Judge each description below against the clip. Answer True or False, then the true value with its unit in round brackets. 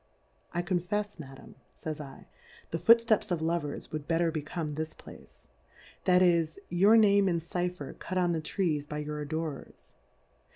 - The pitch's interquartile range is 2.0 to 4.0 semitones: True (3.0 semitones)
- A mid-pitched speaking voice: True (170 Hz)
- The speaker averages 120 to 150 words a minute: False (165 wpm)